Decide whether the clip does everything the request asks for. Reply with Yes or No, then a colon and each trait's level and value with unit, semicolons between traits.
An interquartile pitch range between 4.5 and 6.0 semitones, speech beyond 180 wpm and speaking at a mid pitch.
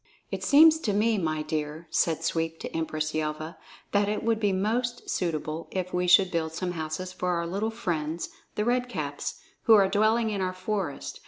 Yes: average, 5.0 semitones; average, 190 wpm; medium, 180 Hz